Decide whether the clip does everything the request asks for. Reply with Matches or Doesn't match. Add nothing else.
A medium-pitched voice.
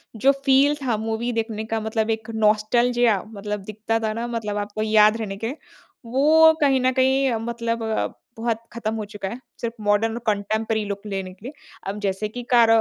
Doesn't match